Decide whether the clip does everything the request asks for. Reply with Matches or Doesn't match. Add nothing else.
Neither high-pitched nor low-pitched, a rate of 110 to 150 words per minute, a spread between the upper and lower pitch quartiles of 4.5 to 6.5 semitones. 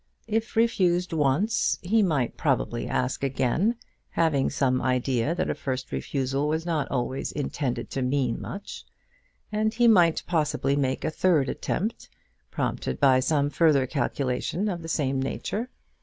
Matches